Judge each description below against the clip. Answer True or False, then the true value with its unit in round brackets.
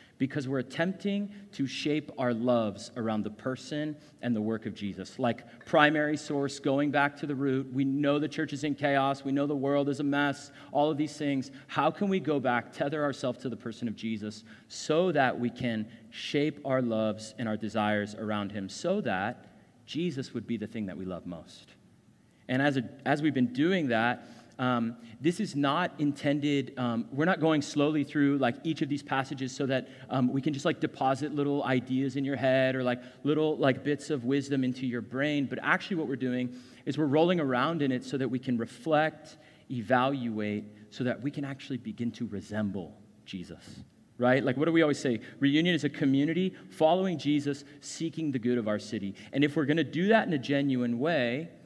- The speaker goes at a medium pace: False (210 wpm)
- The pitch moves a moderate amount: True (3.7 semitones)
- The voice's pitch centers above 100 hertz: True (135 Hz)